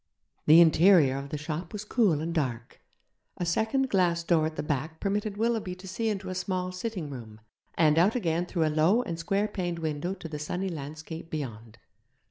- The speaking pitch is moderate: Yes, medium, 170 Hz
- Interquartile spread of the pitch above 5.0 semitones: No, average, 3.9 semitones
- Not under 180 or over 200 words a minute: Yes, average, 195 wpm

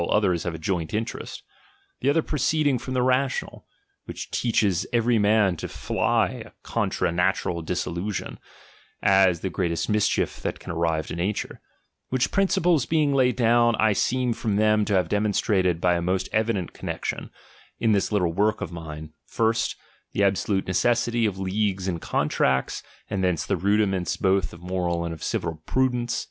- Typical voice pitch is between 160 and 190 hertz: No, low, 100 Hz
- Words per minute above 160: Yes, average, 170 wpm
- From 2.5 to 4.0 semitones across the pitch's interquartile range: No, average, 4.8 semitones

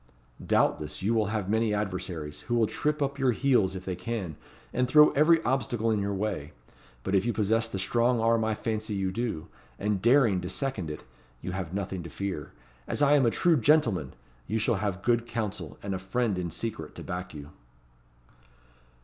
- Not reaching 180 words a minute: No, average, 195 wpm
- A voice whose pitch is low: Yes, low, 105 Hz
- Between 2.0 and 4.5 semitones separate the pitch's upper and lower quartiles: Yes, average, 4.1 semitones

